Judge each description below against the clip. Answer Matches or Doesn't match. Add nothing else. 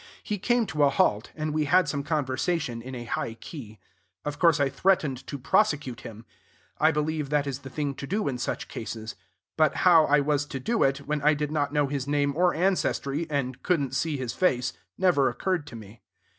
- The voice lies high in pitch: Doesn't match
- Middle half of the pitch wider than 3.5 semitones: Doesn't match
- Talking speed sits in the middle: Doesn't match